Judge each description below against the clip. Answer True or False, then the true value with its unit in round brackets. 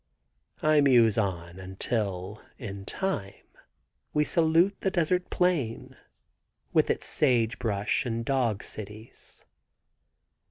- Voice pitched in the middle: False (115 Hz)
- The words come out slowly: True (105 wpm)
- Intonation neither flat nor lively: False (7.3 semitones)